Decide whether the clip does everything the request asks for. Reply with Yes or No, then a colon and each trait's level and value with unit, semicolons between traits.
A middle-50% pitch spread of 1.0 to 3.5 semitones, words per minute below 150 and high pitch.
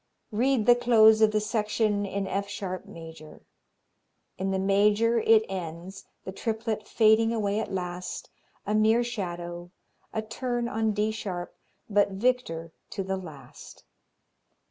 Yes: average, 2.8 semitones; average, 140 wpm; high, 210 Hz